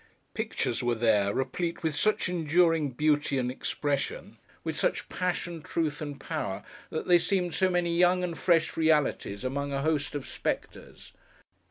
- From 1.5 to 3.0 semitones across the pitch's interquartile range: No, average, 4.0 semitones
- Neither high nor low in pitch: Yes, medium, 155 Hz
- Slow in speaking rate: No, average, 155 wpm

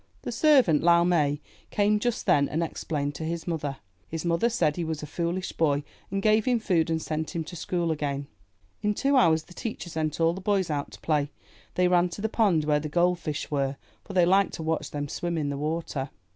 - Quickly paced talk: Yes, fast, 230 wpm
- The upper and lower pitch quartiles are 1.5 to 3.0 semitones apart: No, average, 3.4 semitones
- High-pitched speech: No, medium, 165 Hz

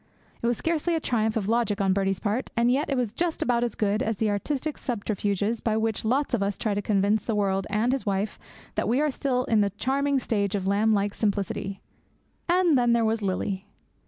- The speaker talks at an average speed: No, fast, 220 wpm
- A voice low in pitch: No, high, 220 Hz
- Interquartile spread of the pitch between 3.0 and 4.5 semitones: Yes, average, 3.7 semitones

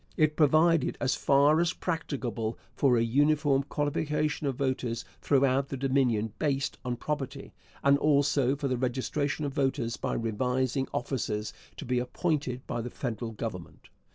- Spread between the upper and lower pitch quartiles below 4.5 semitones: Yes, average, 2.9 semitones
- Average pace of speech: Yes, average, 150 wpm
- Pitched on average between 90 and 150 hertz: Yes, low, 135 Hz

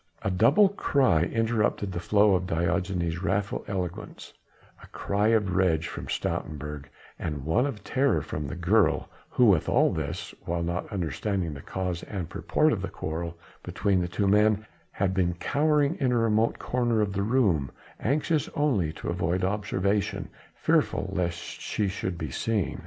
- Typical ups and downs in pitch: Yes, average, 4.2 semitones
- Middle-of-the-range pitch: No, very low, 95 Hz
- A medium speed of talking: Yes, average, 160 wpm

